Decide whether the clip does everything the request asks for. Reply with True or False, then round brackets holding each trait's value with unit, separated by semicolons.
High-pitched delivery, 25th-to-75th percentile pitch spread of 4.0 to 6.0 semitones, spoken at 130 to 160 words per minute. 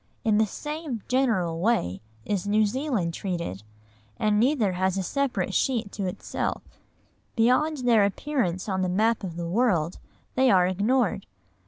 True (210 Hz; 5.3 semitones; 150 wpm)